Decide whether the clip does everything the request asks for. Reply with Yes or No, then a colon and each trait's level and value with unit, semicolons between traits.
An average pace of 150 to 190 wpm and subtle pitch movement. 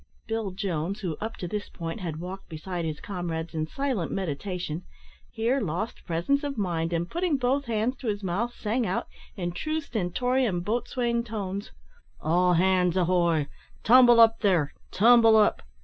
No: average, 160 wpm; average, 5.2 semitones